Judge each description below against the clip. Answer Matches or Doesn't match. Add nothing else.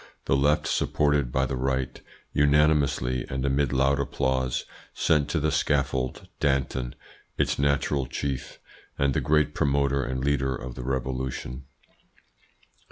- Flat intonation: Matches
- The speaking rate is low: Matches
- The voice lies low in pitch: Matches